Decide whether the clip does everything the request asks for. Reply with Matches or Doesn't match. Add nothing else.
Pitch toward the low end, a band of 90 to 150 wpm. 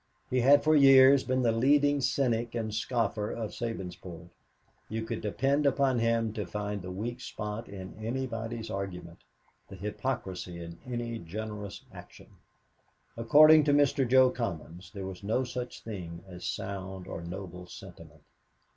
Matches